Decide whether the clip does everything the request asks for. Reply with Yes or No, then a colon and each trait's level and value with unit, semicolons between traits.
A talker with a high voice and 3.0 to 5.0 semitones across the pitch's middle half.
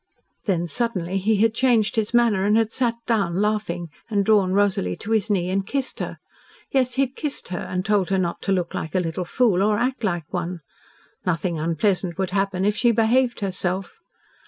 Yes: high, 200 Hz; average, 3.7 semitones